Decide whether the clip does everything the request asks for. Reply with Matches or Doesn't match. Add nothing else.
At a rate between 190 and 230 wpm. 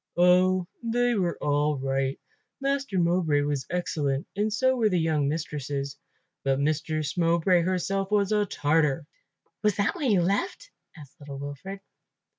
Doesn't match